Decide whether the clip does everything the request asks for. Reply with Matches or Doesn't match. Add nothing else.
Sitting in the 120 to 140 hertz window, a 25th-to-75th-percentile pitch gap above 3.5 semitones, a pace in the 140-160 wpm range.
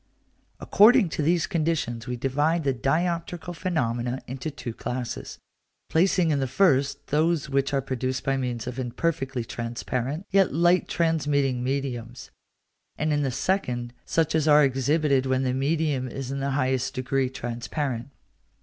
Matches